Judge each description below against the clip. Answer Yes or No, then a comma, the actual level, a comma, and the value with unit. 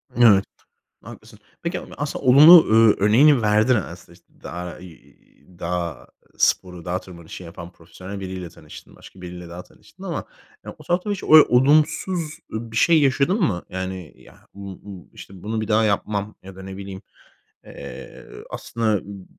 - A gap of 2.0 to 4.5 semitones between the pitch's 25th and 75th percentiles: No, wide, 5.4 semitones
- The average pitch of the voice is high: No, low, 100 Hz